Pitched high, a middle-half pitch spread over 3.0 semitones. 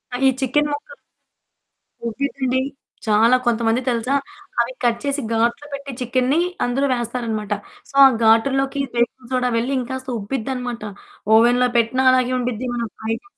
No: very high, 250 Hz; narrow, 2.5 semitones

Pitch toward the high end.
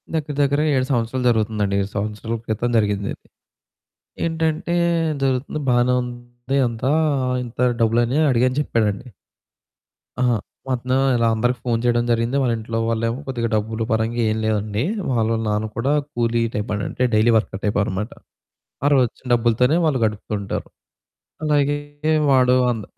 No: low, 120 Hz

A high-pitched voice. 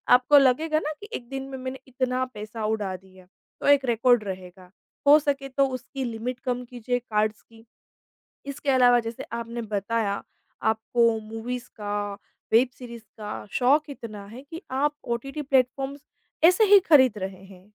Yes: high, 245 Hz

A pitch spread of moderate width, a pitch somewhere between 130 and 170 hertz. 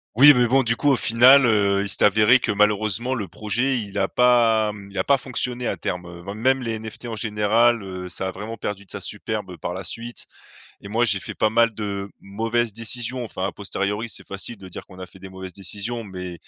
No: average, 3.3 semitones; low, 110 Hz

